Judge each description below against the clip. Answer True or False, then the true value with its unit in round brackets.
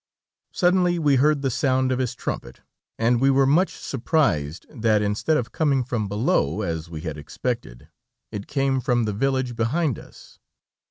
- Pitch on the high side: False (125 Hz)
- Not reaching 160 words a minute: False (165 wpm)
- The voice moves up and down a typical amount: True (4.7 semitones)